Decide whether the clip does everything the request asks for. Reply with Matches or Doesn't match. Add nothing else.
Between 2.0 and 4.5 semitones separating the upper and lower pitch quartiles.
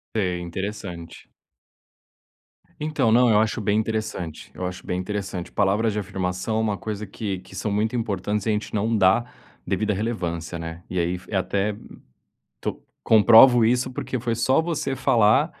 Matches